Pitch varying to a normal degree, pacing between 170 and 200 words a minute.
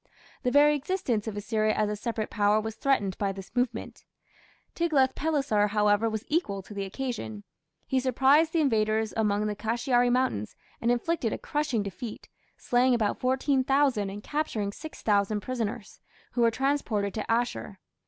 No: average, 4.2 semitones; average, 155 wpm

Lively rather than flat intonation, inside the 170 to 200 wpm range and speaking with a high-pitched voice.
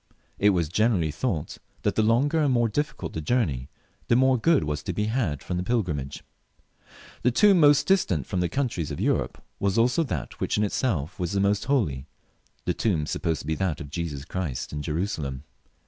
No: wide, 8.0 semitones; average, 180 wpm; very low, 95 Hz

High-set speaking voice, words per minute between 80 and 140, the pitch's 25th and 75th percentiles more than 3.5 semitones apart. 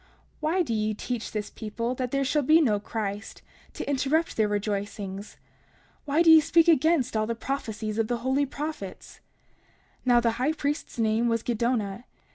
No: high, 240 Hz; average, 175 wpm; average, 4.9 semitones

